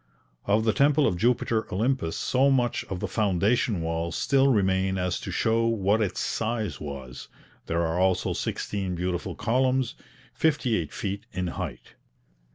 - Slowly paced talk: No, average, 155 wpm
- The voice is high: No, low, 105 Hz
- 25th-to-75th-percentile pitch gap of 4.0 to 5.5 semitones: Yes, average, 4.9 semitones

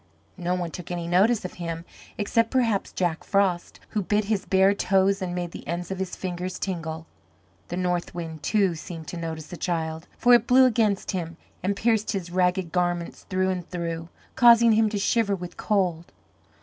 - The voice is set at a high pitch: No, medium, 180 Hz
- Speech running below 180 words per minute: No, average, 190 wpm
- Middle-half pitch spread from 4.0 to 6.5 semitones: No, average, 2.8 semitones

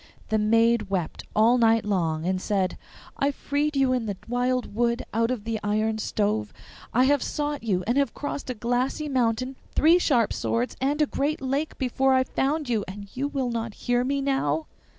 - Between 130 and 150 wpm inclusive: No, average, 190 wpm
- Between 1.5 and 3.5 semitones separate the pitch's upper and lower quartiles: No, average, 4.0 semitones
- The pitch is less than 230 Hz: No, high, 245 Hz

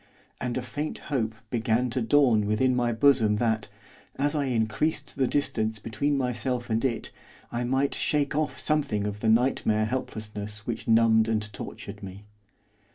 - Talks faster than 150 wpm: Yes, average, 160 wpm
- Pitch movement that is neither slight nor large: Yes, average, 3.4 semitones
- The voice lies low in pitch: Yes, low, 115 Hz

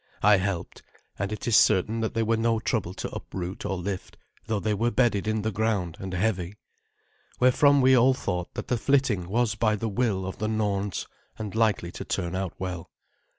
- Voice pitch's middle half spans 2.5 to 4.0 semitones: Yes, average, 3.2 semitones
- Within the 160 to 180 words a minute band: No, average, 195 wpm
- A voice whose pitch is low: Yes, low, 105 Hz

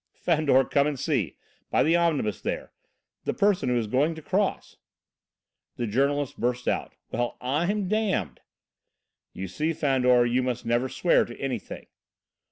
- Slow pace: No, average, 150 wpm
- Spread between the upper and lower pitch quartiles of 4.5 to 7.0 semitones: Yes, average, 4.8 semitones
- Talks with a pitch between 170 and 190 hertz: No, low, 135 Hz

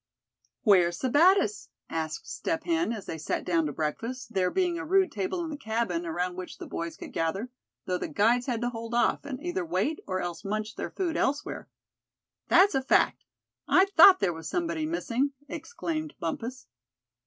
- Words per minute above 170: Yes, average, 180 wpm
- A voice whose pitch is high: Yes, high, 245 Hz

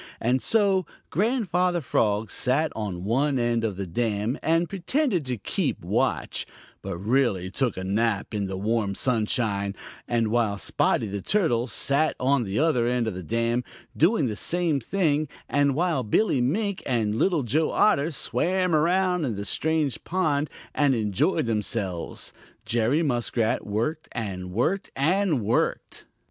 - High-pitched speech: No, low, 125 Hz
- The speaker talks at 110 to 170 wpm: Yes, average, 155 wpm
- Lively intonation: Yes, wide, 6.9 semitones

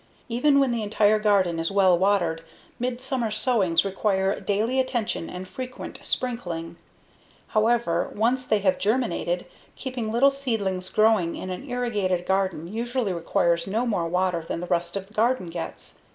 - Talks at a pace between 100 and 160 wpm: Yes, average, 150 wpm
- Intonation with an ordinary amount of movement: Yes, average, 4.9 semitones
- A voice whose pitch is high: Yes, high, 205 Hz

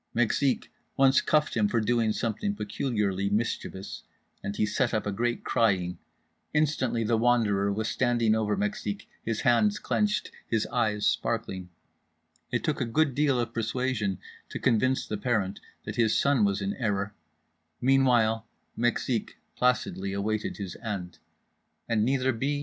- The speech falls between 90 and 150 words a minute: Yes, average, 140 wpm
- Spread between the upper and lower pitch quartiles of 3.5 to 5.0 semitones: Yes, average, 3.8 semitones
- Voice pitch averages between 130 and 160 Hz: No, low, 115 Hz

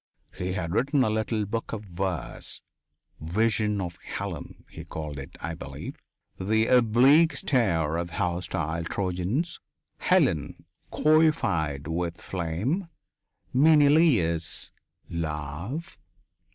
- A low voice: Yes, very low, 95 Hz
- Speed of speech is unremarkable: No, slow, 105 wpm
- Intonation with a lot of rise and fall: Yes, wide, 7.1 semitones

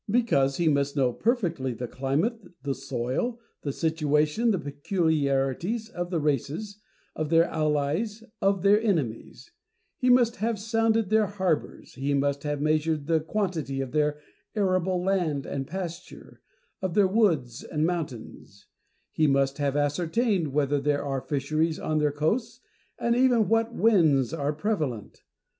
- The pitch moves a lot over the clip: Yes, wide, 6.2 semitones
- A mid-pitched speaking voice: Yes, medium, 155 Hz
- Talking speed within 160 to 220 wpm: No, average, 145 wpm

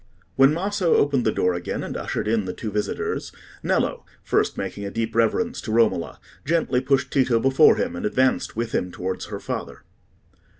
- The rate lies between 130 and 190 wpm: Yes, average, 180 wpm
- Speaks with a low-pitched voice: Yes, low, 120 Hz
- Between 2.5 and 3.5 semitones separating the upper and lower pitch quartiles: No, average, 5.0 semitones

